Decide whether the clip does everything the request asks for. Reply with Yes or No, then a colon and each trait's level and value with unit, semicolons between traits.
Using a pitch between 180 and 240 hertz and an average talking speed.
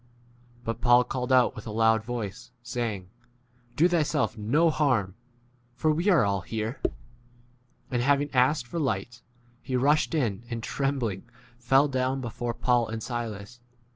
No: low, 120 Hz; average, 155 wpm